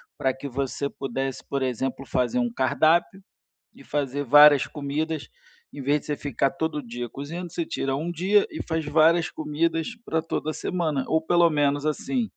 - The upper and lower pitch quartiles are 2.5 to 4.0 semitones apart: Yes, average, 3.0 semitones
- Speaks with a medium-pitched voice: Yes, medium, 150 Hz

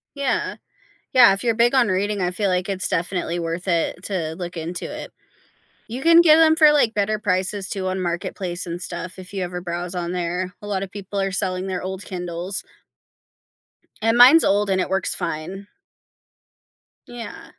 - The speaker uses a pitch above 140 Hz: Yes, high, 190 Hz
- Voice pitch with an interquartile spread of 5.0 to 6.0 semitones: No, average, 2.7 semitones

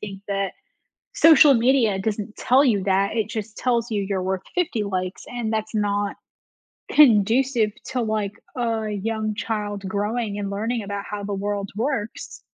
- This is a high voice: Yes, high, 215 Hz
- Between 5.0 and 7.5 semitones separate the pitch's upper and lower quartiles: No, narrow, 2.5 semitones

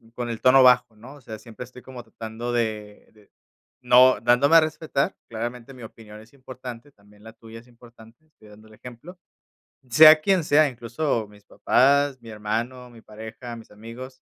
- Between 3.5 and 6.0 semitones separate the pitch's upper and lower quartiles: No, average, 2.7 semitones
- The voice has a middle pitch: No, low, 120 Hz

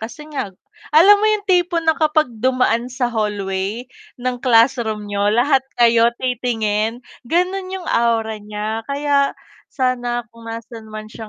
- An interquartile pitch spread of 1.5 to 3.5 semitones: No, average, 4.3 semitones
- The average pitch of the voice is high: Yes, high, 240 Hz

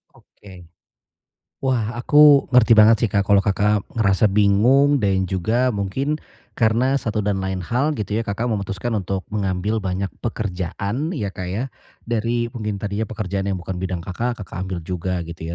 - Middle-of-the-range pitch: No, low, 105 Hz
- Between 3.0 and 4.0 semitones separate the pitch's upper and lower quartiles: Yes, average, 3.6 semitones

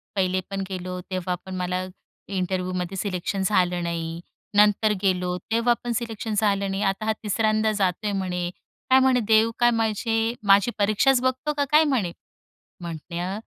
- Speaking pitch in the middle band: No, high, 200 Hz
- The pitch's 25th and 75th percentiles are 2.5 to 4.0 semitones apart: Yes, average, 3.6 semitones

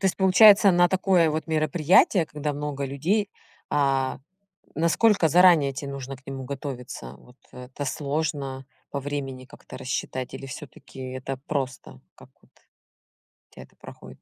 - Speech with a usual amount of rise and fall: Yes, average, 3.7 semitones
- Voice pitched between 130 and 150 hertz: Yes, medium, 140 Hz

